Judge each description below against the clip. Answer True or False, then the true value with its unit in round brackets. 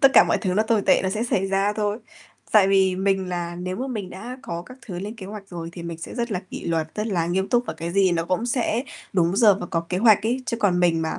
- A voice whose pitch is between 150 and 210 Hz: True (195 Hz)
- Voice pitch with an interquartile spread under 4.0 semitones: True (3.5 semitones)